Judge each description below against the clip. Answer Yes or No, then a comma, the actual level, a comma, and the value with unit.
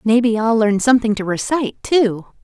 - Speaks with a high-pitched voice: Yes, high, 225 Hz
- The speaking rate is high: No, average, 195 wpm